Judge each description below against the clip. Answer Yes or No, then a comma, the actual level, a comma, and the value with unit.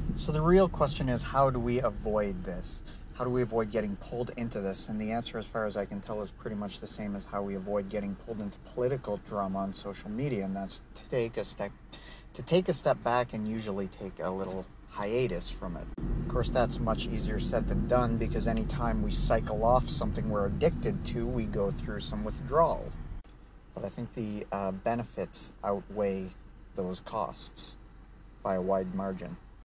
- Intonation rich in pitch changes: No, average, 3.7 semitones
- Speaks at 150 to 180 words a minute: No, average, 200 wpm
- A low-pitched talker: Yes, low, 105 Hz